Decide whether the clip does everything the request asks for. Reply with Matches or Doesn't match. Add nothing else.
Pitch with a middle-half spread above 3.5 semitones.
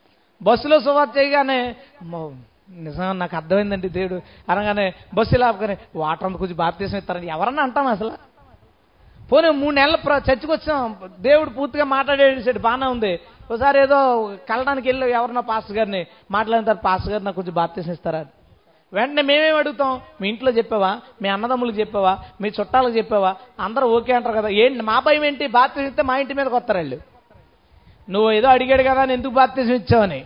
Matches